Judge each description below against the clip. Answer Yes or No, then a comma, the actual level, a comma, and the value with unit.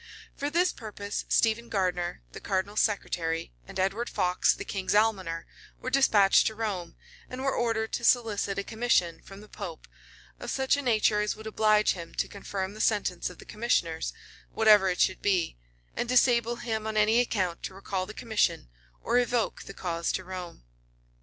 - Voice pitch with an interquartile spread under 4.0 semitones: Yes, average, 3.5 semitones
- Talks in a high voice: Yes, high, 210 Hz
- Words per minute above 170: Yes, average, 180 wpm